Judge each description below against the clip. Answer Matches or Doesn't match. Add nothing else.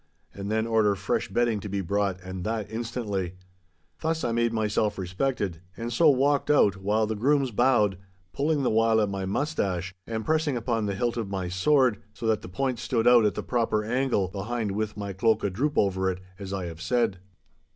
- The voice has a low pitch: Matches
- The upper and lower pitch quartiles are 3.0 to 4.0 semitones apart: Matches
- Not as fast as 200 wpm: Doesn't match